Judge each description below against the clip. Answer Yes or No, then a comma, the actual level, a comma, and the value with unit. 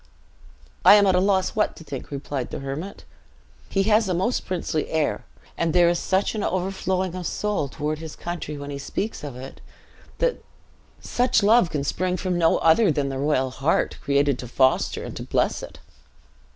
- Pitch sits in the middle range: Yes, medium, 170 Hz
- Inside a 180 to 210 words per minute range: Yes, average, 190 wpm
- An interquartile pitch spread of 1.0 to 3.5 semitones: No, average, 5.1 semitones